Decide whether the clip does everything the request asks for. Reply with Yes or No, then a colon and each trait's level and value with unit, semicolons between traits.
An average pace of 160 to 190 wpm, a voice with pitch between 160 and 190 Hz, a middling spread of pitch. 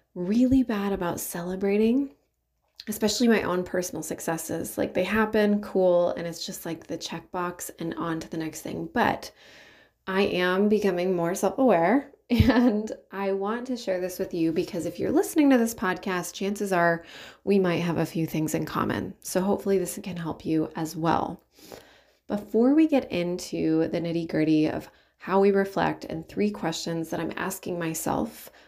Yes: average, 175 wpm; medium, 185 Hz; average, 3.7 semitones